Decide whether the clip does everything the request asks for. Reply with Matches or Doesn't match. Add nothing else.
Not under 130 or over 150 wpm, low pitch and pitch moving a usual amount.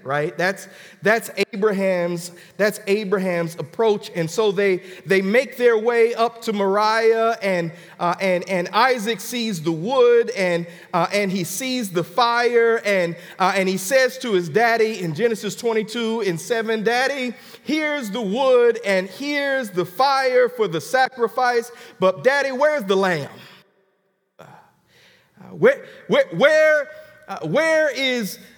Doesn't match